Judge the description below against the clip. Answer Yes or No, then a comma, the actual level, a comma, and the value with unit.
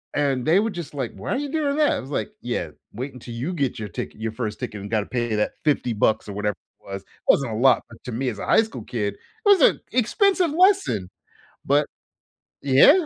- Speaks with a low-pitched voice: Yes, low, 130 Hz